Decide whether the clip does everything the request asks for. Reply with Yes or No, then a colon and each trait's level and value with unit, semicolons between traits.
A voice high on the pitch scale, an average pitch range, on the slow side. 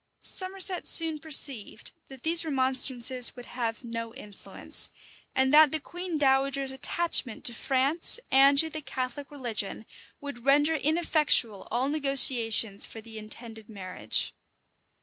Yes: very high, 265 Hz; average, 4.6 semitones; slow, 130 wpm